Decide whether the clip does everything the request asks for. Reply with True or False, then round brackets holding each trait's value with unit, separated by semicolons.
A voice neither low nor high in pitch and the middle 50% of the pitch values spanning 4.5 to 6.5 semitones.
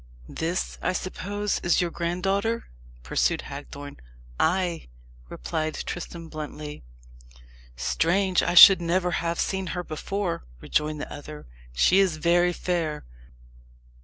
False (170 Hz; 3.2 semitones)